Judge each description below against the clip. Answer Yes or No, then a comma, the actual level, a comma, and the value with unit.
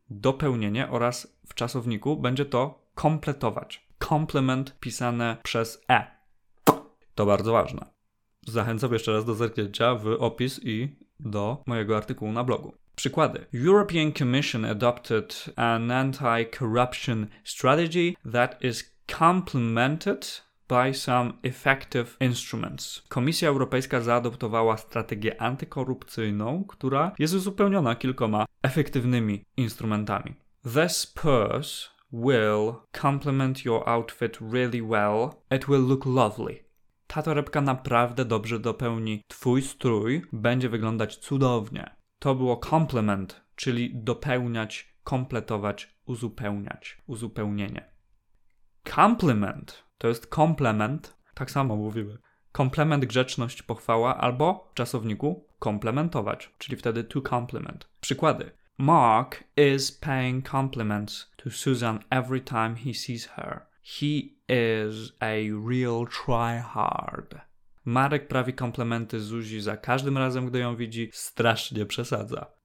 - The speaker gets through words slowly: Yes, slow, 105 wpm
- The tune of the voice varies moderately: Yes, average, 3.1 semitones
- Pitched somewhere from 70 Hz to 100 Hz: No, low, 120 Hz